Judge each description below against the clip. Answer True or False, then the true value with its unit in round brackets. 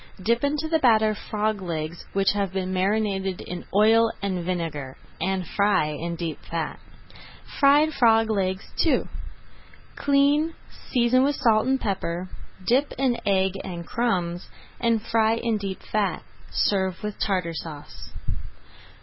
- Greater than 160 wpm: False (135 wpm)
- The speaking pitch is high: True (200 Hz)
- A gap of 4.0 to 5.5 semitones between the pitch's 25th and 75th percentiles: True (4.3 semitones)